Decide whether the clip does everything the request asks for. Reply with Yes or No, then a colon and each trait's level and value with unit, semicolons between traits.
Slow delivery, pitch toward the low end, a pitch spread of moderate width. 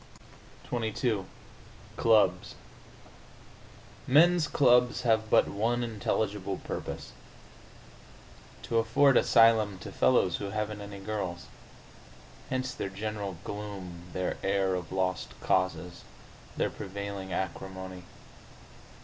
Yes: slow, 95 wpm; low, 100 Hz; average, 3.3 semitones